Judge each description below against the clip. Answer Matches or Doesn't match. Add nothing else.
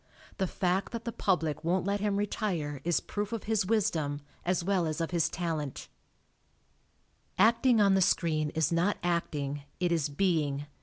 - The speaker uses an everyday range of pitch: Matches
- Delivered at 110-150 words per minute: Doesn't match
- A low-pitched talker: Doesn't match